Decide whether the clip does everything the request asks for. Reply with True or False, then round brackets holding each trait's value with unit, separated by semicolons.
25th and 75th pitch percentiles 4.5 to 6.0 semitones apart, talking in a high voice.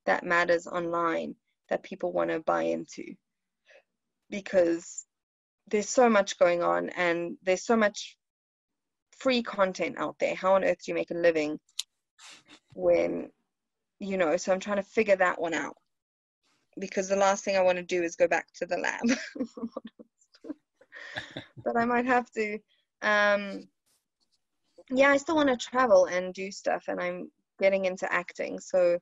True (4.9 semitones; 195 Hz)